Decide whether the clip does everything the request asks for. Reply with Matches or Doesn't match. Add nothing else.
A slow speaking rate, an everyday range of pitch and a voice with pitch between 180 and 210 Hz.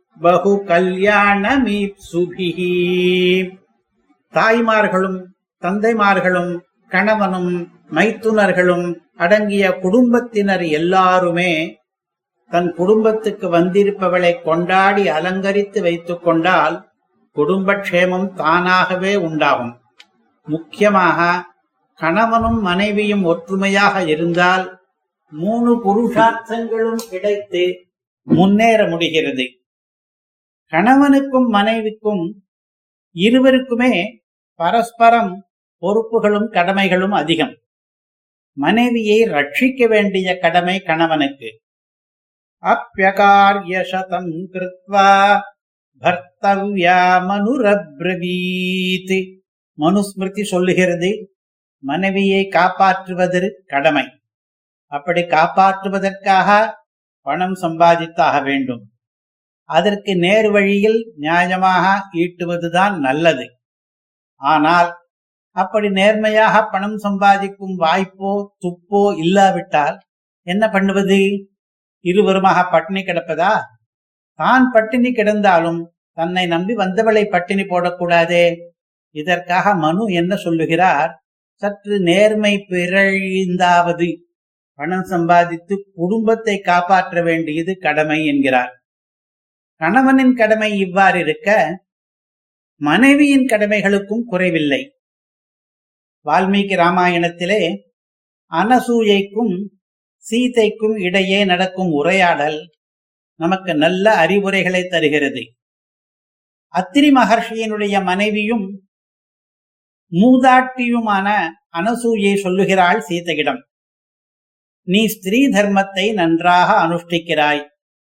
Matches